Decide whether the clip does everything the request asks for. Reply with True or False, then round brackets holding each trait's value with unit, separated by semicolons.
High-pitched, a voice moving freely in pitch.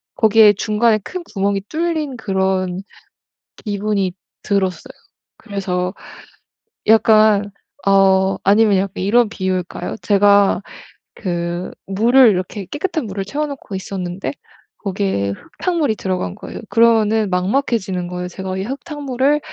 False (200 Hz; 3.1 semitones)